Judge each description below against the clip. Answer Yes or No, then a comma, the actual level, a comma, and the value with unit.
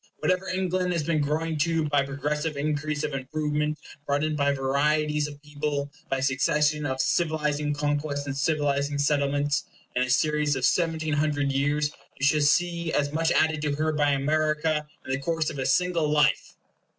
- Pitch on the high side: No, medium, 150 Hz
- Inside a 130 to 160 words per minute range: No, average, 175 wpm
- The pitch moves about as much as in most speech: No, narrow, 1.4 semitones